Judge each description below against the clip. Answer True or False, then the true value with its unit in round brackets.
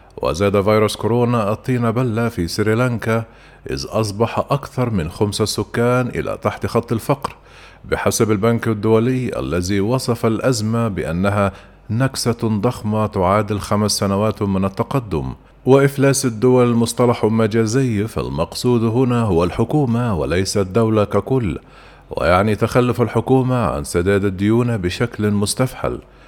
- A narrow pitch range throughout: False (3.2 semitones)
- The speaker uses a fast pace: False (115 wpm)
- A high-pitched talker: False (115 Hz)